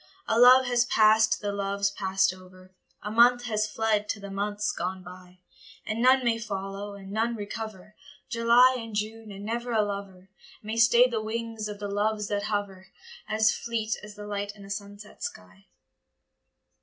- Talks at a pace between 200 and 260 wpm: No, average, 180 wpm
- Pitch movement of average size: No, narrow, 2.1 semitones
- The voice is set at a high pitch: Yes, high, 210 Hz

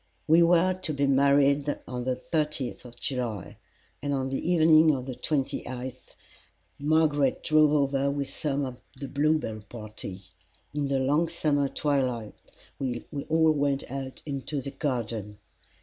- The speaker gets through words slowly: No, average, 150 wpm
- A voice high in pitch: No, medium, 140 Hz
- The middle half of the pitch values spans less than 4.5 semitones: Yes, average, 2.8 semitones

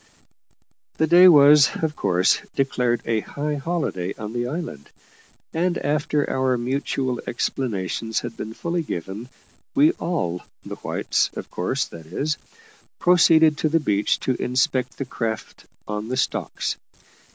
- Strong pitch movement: Yes, wide, 5.7 semitones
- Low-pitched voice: Yes, low, 130 Hz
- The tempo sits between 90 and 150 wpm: Yes, average, 140 wpm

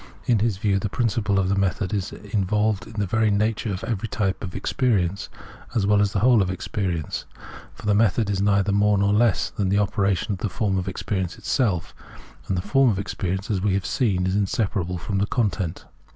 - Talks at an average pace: No, fast, 220 wpm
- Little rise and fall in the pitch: Yes, narrow, 2.0 semitones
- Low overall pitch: Yes, low, 100 Hz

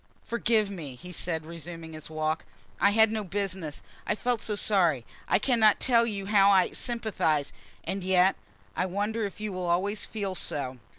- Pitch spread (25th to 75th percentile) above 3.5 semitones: Yes, average, 4.3 semitones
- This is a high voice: Yes, high, 195 Hz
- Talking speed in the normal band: Yes, average, 175 wpm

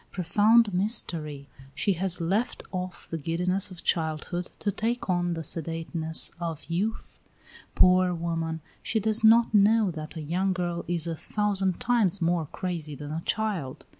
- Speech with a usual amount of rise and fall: Yes, average, 3.7 semitones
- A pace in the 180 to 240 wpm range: No, average, 155 wpm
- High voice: No, medium, 175 Hz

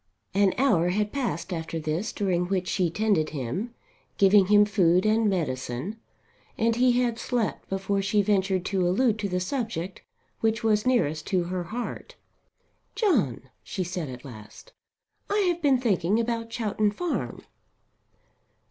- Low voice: No, high, 200 Hz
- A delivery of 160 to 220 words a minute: No, average, 150 wpm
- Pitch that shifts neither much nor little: Yes, average, 4.3 semitones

